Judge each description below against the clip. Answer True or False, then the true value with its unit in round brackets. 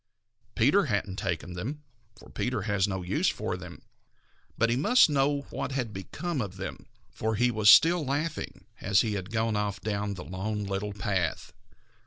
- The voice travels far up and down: False (4.8 semitones)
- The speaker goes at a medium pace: True (175 wpm)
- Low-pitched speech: True (105 Hz)